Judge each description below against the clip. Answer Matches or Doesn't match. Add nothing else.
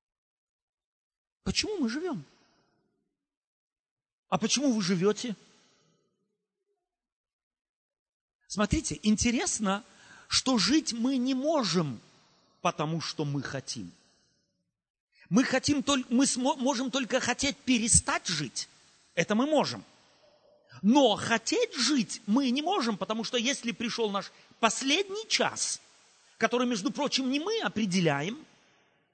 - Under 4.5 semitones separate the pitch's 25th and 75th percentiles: Doesn't match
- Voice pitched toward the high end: Matches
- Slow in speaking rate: Matches